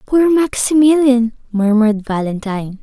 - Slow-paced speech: Yes, slow, 85 wpm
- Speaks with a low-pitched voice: No, high, 240 Hz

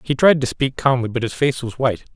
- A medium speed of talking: No, fast, 280 wpm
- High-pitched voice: No, low, 130 Hz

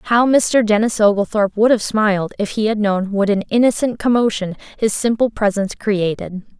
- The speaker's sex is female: Yes, female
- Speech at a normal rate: Yes, average, 175 wpm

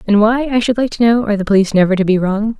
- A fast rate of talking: Yes, fast, 325 wpm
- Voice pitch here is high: Yes, high, 215 Hz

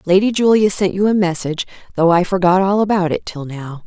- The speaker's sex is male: No, female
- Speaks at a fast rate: Yes, fast, 215 wpm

